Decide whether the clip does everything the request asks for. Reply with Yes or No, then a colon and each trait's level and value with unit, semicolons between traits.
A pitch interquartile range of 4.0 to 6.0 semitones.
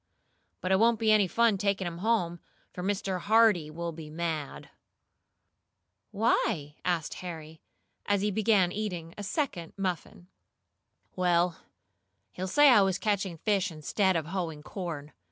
No: average, 3.5 semitones